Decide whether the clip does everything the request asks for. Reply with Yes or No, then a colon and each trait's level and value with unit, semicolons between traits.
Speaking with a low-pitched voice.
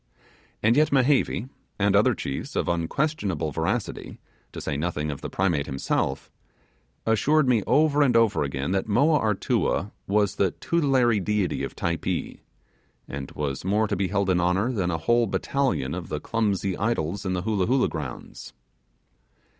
Yes: low, 100 Hz